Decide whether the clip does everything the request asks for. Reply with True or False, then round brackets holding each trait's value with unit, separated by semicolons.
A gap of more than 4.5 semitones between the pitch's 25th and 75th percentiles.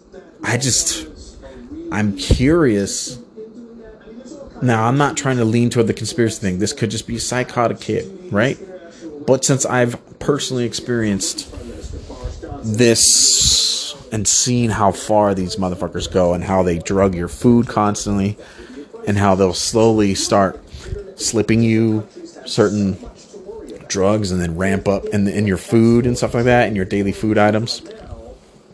False (3.7 semitones)